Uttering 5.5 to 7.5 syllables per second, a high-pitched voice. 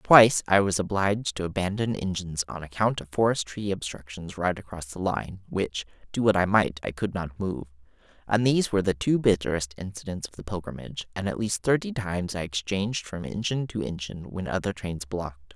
No: 5.6 syllables/s; very low, 95 Hz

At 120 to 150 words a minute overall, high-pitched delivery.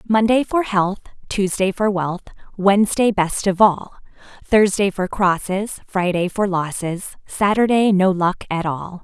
Yes: average, 140 wpm; high, 195 Hz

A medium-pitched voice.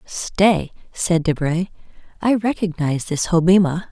Yes: medium, 175 Hz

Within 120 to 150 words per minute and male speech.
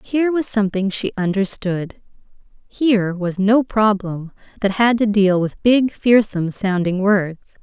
No: average, 140 wpm; female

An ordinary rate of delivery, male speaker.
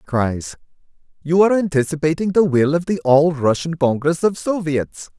Yes: average, 150 wpm; male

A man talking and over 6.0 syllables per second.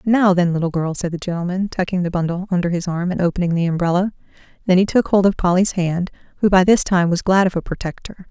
No: female; 6.3 syllables/s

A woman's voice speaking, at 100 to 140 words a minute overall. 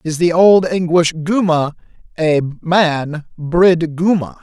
No: male; slow, 135 wpm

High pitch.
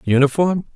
No: medium, 150 Hz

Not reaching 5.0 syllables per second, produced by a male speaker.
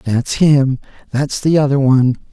Yes: 4.5 syllables/s; male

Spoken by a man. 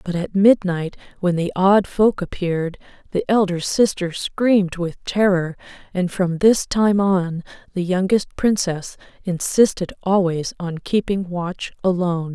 No: female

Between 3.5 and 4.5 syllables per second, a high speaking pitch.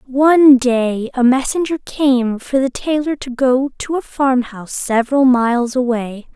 Yes: 4.4 syllables/s; very high, 255 Hz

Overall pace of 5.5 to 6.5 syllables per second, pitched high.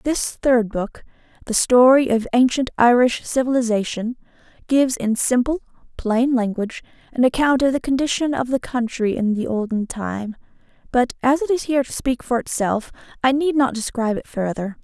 No: 5.2 syllables/s; high, 245 Hz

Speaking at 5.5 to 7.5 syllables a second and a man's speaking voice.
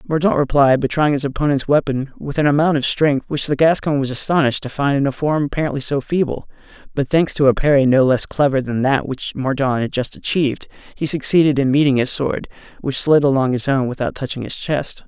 Yes: 5.8 syllables/s; male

